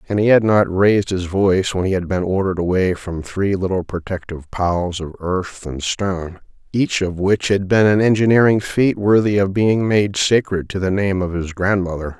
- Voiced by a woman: No, male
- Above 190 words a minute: Yes, average, 200 wpm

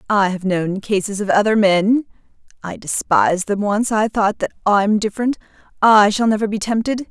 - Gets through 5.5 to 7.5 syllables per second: No, 5.0 syllables/s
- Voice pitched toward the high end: Yes, high, 205 Hz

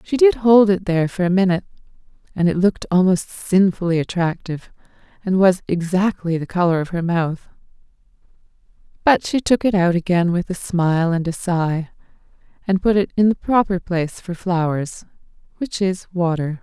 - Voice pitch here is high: No, medium, 180 Hz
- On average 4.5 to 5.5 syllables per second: Yes, 5.3 syllables/s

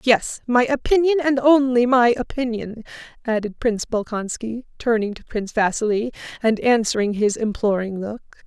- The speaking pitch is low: No, high, 235 Hz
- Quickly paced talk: No, slow, 135 wpm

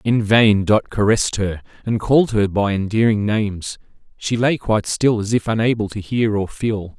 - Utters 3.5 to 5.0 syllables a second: No, 5.2 syllables/s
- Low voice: Yes, low, 105 Hz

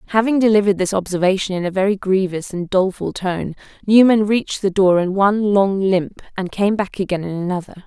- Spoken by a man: No, female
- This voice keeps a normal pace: Yes, average, 190 wpm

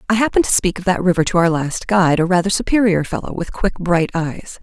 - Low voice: No, medium, 180 Hz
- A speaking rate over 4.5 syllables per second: Yes, 6.1 syllables/s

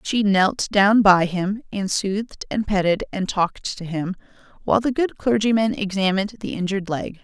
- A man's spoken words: No, female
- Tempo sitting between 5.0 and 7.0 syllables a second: Yes, 5.1 syllables/s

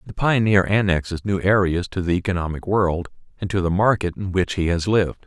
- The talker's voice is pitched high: No, very low, 95 Hz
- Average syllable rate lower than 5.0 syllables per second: No, 5.7 syllables/s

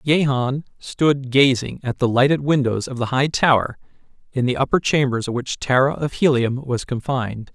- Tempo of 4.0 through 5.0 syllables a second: Yes, 4.9 syllables/s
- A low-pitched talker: Yes, low, 130 Hz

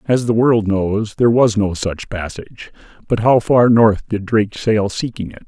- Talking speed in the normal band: Yes, average, 195 wpm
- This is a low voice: Yes, low, 110 Hz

